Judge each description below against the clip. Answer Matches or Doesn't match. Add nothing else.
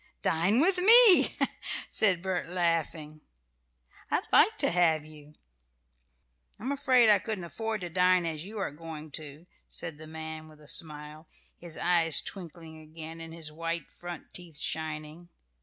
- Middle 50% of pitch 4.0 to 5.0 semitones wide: Doesn't match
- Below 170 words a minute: Matches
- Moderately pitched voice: Matches